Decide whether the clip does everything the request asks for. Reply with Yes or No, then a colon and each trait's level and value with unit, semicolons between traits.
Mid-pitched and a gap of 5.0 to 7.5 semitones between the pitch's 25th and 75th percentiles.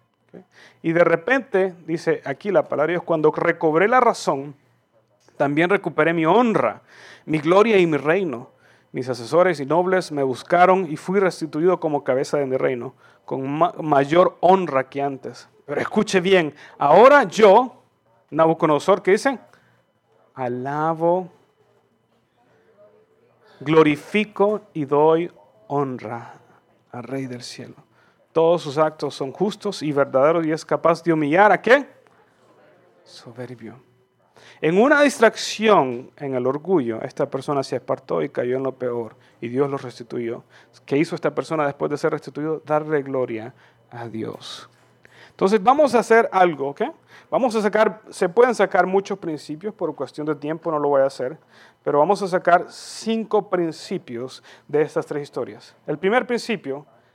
Yes: medium, 155 Hz; wide, 5.6 semitones